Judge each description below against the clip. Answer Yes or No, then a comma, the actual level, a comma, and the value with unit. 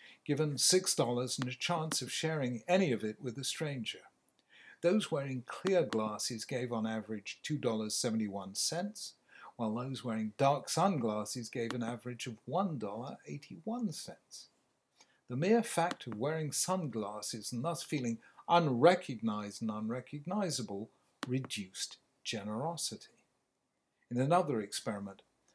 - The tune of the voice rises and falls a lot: Yes, wide, 6.8 semitones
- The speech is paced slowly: Yes, slow, 115 wpm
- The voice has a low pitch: Yes, low, 125 Hz